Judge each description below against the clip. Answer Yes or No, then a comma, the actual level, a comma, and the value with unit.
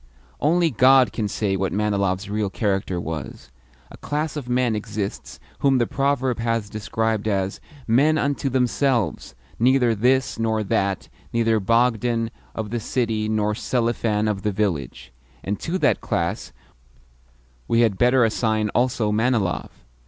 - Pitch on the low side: Yes, low, 110 Hz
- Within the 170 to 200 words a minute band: No, average, 140 wpm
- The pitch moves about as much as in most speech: Yes, average, 3.2 semitones